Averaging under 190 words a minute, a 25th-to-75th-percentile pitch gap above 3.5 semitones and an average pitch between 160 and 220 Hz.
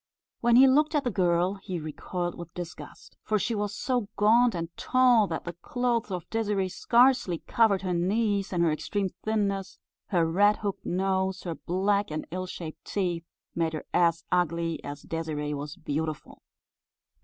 Yes: average, 165 wpm; average, 3.9 semitones; medium, 185 Hz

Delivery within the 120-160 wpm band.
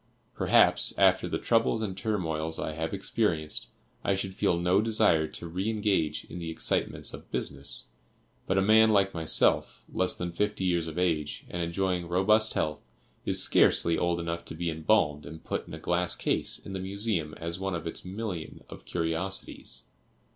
No: average, 175 wpm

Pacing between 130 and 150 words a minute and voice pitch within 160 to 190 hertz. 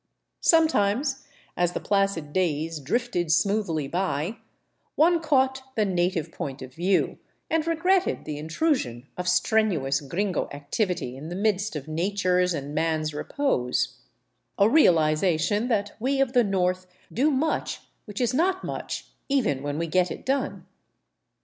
Yes: average, 140 wpm; medium, 185 Hz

